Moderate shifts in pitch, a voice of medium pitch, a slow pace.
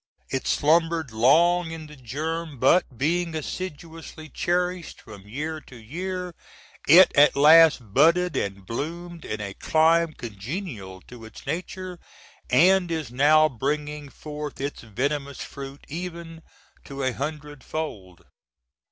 Yes: average, 4.2 semitones; medium, 150 Hz; slow, 125 wpm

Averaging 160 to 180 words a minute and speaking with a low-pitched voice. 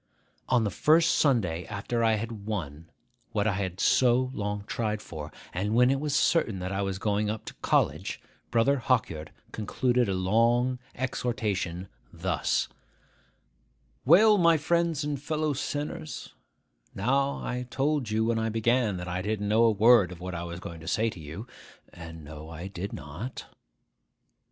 Yes: average, 165 wpm; low, 110 Hz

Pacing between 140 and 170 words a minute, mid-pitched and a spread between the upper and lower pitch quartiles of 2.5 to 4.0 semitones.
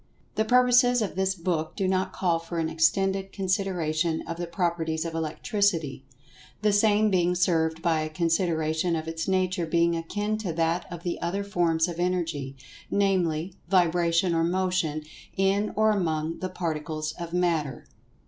Yes: average, 160 wpm; medium, 175 Hz; average, 2.9 semitones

